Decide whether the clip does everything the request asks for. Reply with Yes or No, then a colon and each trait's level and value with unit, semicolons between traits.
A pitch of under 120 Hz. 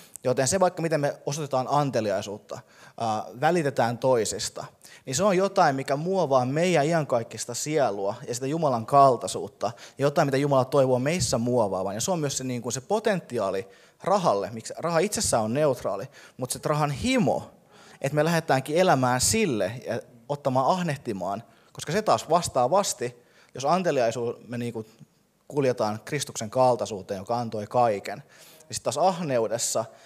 No: low, 130 Hz